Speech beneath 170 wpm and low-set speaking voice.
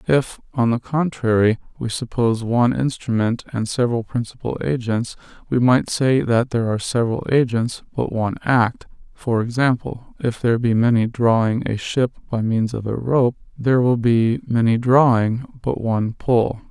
Yes: average, 160 wpm; low, 120 Hz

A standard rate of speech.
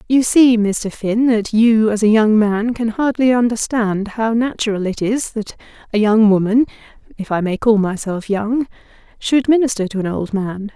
Yes: average, 175 wpm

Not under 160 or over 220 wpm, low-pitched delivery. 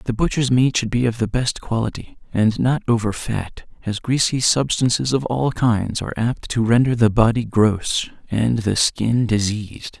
Yes: average, 180 wpm; low, 115 Hz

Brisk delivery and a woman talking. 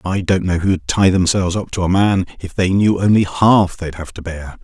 No: fast, 245 wpm; male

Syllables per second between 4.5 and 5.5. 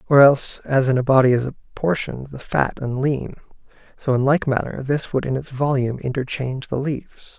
Yes: 5.4 syllables/s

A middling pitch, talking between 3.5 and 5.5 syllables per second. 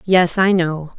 Yes: medium, 175 Hz; 3.6 syllables/s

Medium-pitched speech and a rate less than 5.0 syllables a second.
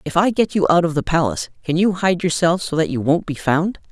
No: medium, 170 Hz; 5.9 syllables/s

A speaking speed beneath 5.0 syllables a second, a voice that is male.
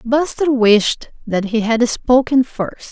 No: 3.4 syllables/s; female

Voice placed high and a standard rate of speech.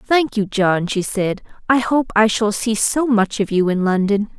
No: high, 215 Hz; fast, 220 wpm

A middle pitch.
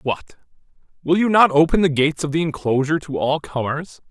Yes: medium, 150 Hz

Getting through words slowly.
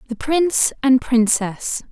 Yes: slow, 125 wpm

